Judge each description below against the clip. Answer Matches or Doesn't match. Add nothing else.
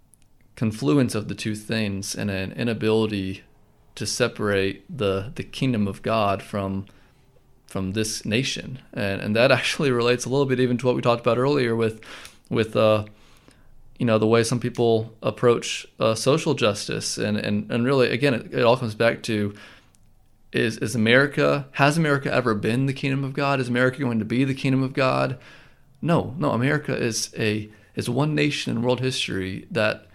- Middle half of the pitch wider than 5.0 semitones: Doesn't match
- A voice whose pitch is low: Matches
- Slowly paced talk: Doesn't match